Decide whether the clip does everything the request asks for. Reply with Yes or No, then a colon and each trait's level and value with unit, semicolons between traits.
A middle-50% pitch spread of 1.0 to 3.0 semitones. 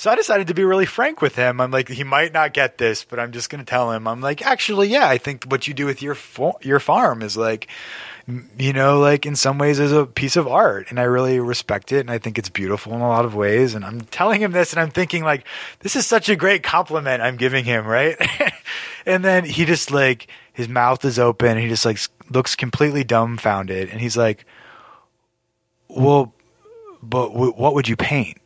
No: average, 4.3 semitones